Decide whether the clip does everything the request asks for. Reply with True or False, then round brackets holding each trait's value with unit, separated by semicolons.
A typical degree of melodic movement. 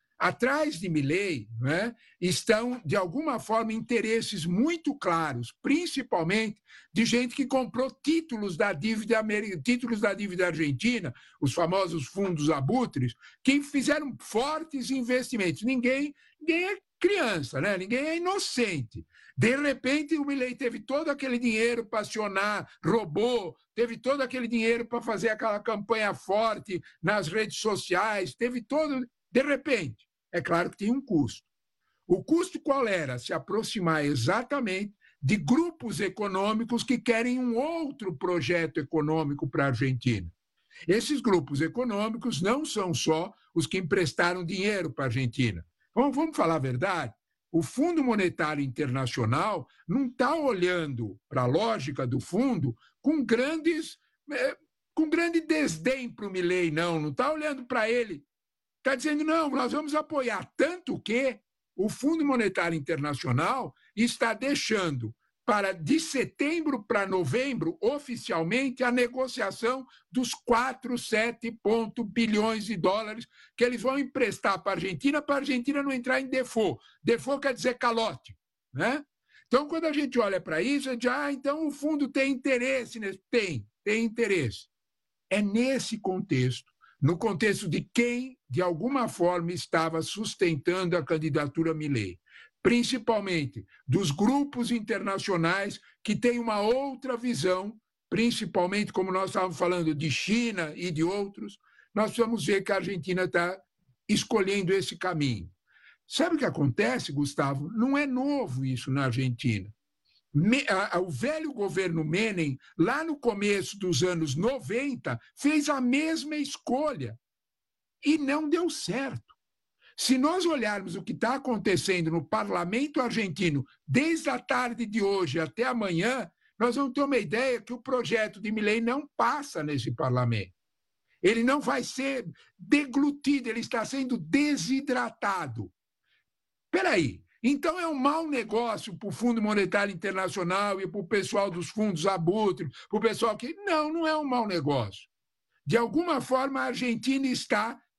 False (6.7 semitones)